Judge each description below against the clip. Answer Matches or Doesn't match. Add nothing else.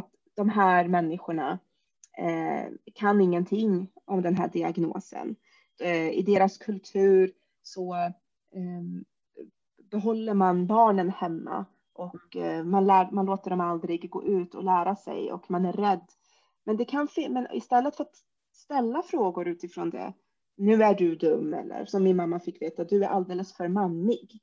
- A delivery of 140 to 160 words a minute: Matches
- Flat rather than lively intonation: Doesn't match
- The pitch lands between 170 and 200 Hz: Matches